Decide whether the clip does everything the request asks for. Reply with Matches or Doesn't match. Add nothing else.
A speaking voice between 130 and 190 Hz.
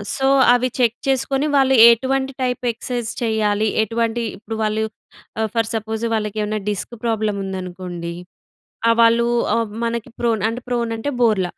Doesn't match